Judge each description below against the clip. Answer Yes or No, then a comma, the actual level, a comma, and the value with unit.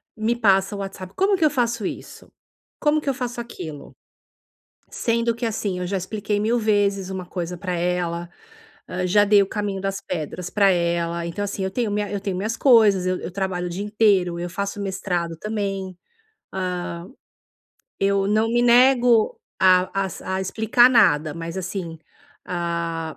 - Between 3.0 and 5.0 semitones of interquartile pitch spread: Yes, average, 3.3 semitones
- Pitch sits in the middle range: No, high, 195 Hz